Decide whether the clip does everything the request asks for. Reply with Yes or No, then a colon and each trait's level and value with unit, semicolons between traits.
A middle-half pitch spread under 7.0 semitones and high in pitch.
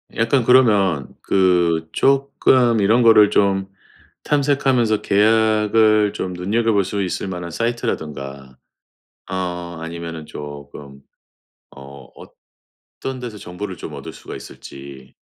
No: wide, 5.6 semitones; very low, 95 Hz